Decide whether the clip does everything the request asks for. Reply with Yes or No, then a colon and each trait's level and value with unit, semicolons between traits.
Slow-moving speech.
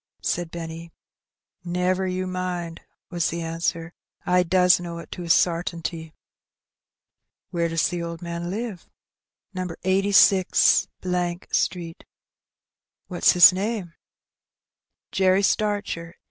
Yes: slow, 110 wpm